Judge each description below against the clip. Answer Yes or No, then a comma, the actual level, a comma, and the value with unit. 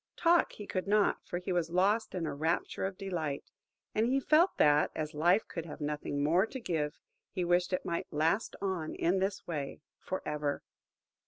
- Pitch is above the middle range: No, medium, 175 Hz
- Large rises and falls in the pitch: No, average, 4.2 semitones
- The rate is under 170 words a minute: No, average, 190 wpm